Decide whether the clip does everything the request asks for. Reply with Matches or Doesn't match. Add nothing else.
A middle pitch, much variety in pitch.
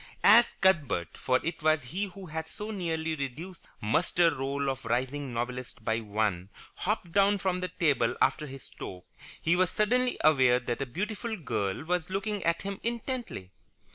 Matches